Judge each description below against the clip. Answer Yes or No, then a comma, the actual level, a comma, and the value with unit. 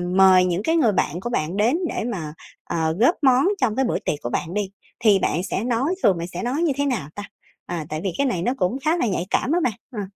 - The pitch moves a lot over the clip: Yes, wide, 6.3 semitones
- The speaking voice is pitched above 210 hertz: No, high, 205 Hz